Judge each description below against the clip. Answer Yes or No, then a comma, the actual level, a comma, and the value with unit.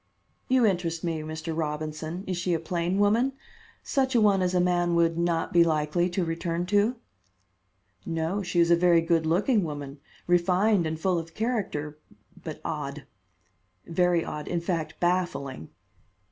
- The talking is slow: No, average, 160 wpm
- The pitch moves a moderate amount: No, narrow, 2.3 semitones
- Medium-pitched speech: Yes, medium, 170 Hz